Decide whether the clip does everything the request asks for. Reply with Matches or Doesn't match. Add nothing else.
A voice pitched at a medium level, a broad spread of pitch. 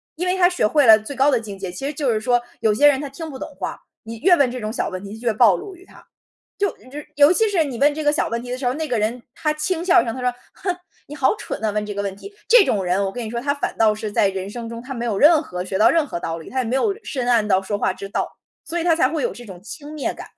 Doesn't match